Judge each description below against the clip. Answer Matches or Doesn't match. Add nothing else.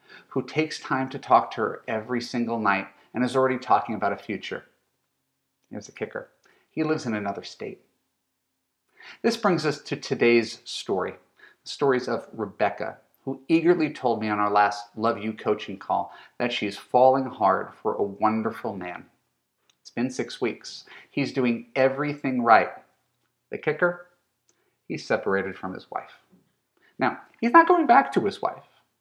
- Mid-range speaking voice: Doesn't match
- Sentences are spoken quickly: Doesn't match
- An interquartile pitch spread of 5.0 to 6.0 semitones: Matches